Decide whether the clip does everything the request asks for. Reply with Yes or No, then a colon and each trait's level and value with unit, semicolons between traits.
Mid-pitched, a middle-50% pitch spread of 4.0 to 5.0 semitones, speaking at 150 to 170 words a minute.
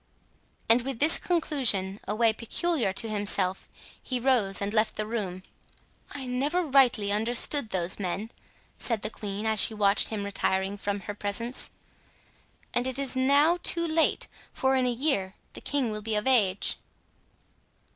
No: high, 225 Hz; average, 4.6 semitones; average, 155 wpm